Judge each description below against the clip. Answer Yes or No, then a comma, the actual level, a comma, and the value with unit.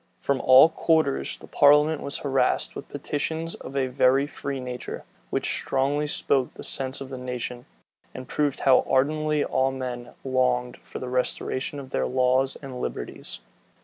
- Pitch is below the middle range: Yes, low, 130 Hz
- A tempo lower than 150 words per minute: No, average, 160 wpm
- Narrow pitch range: Yes, narrow, 2.0 semitones